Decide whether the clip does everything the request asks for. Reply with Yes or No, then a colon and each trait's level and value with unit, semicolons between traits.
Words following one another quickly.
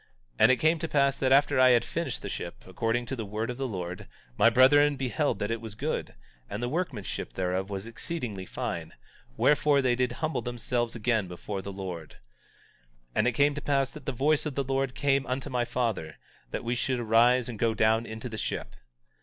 Yes: fast, 220 wpm